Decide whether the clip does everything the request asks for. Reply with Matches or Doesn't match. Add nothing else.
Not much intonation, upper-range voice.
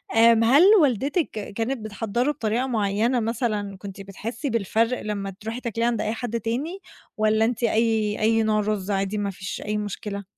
Matches